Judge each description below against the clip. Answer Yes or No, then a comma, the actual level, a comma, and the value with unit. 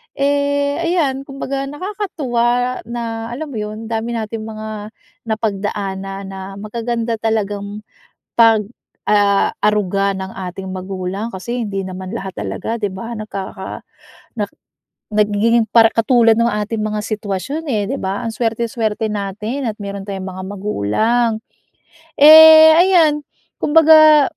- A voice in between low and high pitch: No, high, 220 Hz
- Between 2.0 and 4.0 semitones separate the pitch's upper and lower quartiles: Yes, average, 3.6 semitones